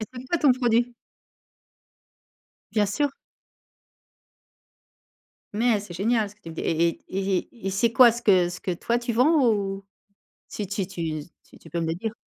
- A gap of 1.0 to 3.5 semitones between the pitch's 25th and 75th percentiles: No, average, 4.4 semitones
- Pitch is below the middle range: No, high, 210 Hz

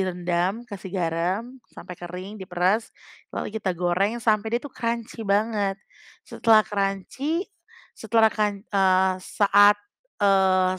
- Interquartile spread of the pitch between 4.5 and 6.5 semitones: No, average, 2.9 semitones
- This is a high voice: Yes, high, 200 Hz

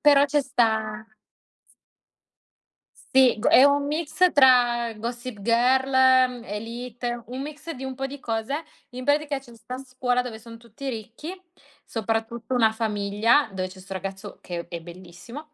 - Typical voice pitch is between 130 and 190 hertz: No, high, 240 Hz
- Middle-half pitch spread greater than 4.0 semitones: No, average, 3.2 semitones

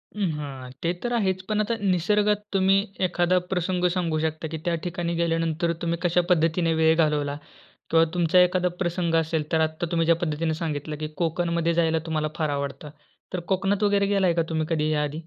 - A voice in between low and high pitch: Yes, medium, 170 Hz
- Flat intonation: Yes, narrow, 2.3 semitones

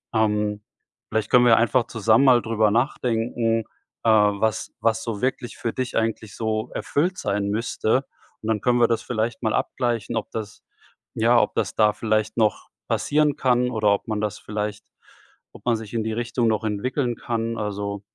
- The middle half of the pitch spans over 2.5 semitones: No, narrow, 2.0 semitones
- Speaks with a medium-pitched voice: No, low, 110 Hz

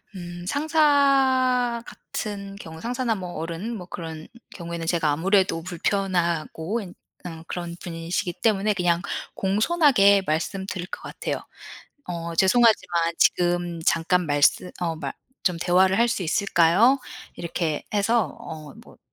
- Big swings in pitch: No, average, 4.1 semitones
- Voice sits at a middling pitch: Yes, medium, 180 Hz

